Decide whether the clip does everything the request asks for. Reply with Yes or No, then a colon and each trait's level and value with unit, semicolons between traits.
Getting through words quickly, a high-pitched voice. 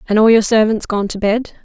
Yes: fast, 255 wpm; high, 215 Hz